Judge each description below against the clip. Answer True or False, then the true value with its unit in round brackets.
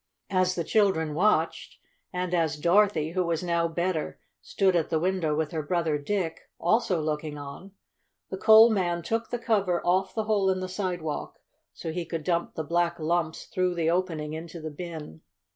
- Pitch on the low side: False (175 Hz)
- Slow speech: False (180 wpm)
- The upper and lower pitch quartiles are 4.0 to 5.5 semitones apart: False (2.8 semitones)